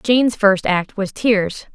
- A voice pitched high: Yes, high, 210 Hz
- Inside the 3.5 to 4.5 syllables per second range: Yes, 3.6 syllables/s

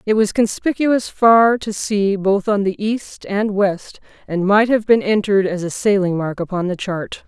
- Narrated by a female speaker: Yes, female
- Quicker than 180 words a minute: Yes, average, 200 wpm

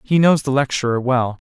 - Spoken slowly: No, fast, 205 wpm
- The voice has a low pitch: Yes, low, 130 Hz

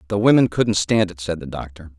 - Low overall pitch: Yes, very low, 95 Hz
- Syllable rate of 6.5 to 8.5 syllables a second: No, 5.8 syllables/s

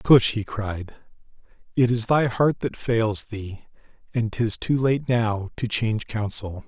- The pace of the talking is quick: No, average, 160 wpm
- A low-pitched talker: Yes, low, 115 Hz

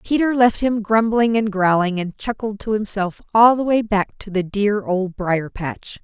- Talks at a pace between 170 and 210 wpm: Yes, average, 200 wpm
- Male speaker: No, female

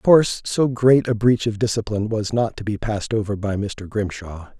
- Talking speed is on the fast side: Yes, fast, 220 wpm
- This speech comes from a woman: No, male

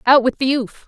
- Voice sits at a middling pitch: No, very high, 255 Hz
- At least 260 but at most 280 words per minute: Yes, fast, 275 wpm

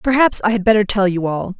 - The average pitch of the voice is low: No, high, 205 Hz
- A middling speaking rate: No, fast, 265 wpm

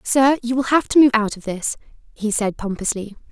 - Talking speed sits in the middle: No, fast, 215 wpm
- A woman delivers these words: Yes, female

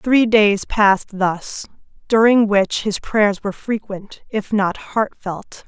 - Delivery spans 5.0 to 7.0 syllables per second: No, 3.5 syllables/s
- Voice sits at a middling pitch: No, high, 205 Hz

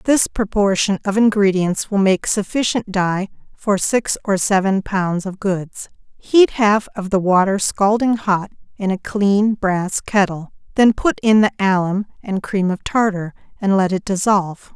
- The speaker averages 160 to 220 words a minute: Yes, average, 165 wpm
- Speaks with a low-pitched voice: No, high, 200 Hz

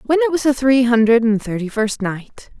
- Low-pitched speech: No, high, 245 Hz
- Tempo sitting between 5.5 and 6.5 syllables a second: No, 5.2 syllables/s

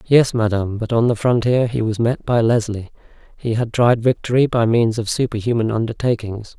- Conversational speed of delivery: Yes, average, 180 wpm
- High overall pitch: No, low, 115 Hz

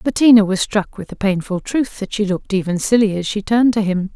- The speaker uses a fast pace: Yes, fast, 245 wpm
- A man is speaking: No, female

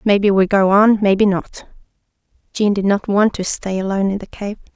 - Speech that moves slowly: No, average, 200 wpm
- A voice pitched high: Yes, high, 200 Hz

